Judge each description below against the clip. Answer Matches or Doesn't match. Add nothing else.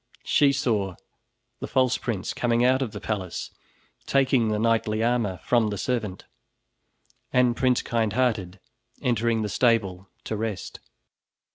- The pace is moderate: Doesn't match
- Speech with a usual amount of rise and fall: Matches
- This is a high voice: Doesn't match